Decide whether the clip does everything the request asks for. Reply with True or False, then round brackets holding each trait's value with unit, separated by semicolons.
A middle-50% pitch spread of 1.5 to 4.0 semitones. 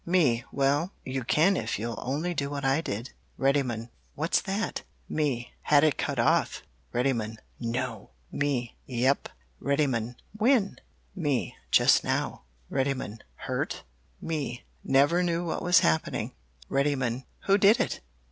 False (4.9 semitones)